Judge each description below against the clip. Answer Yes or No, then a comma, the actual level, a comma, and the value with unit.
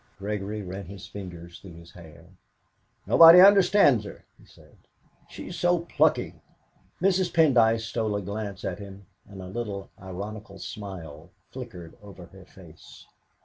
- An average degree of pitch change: Yes, average, 4.0 semitones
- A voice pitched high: No, low, 100 Hz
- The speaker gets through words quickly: No, average, 140 wpm